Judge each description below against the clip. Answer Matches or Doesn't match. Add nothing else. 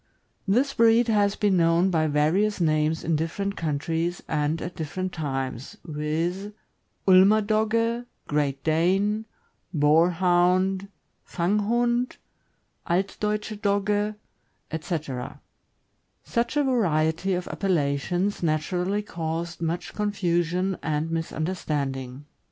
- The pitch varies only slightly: Doesn't match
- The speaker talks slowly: Matches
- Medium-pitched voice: Matches